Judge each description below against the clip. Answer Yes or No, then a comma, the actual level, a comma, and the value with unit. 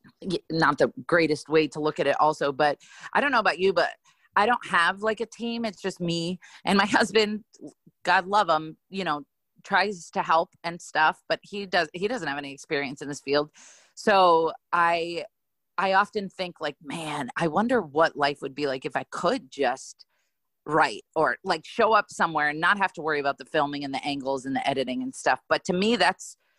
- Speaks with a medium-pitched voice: Yes, medium, 170 Hz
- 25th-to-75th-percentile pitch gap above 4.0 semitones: Yes, average, 5.2 semitones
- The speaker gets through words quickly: Yes, fast, 210 wpm